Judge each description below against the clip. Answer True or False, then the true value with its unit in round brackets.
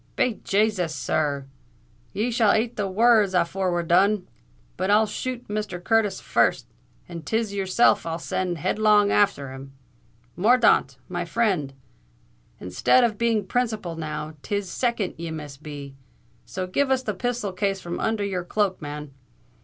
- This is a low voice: False (195 Hz)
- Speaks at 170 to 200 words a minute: False (155 wpm)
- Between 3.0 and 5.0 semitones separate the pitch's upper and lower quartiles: True (4.5 semitones)